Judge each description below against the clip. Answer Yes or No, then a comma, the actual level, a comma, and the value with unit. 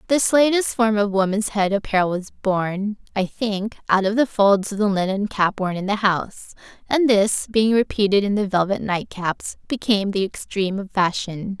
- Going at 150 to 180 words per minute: No, average, 190 wpm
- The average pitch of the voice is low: No, high, 205 Hz